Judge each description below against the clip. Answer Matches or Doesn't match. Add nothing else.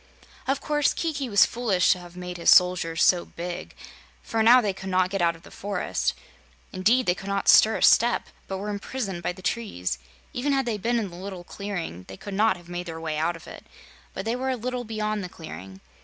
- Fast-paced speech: Matches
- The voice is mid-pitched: Doesn't match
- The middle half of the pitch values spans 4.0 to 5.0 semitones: Matches